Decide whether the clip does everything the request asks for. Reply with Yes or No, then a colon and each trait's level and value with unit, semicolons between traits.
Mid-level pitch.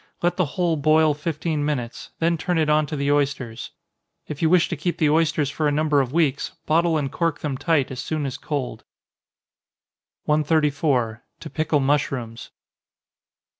Yes: medium, 150 Hz